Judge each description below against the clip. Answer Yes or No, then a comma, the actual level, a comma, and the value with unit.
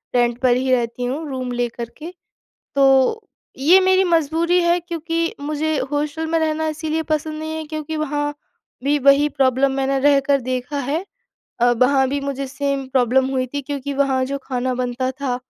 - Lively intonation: No, average, 3.2 semitones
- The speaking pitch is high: Yes, very high, 280 Hz